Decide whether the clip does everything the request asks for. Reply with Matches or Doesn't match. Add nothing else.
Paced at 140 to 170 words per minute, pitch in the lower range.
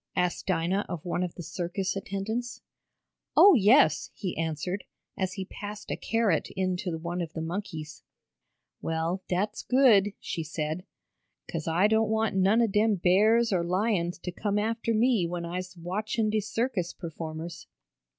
Doesn't match